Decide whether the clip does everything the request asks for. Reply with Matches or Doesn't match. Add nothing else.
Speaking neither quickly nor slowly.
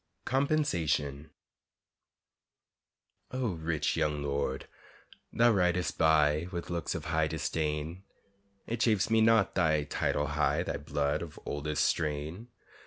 Doesn't match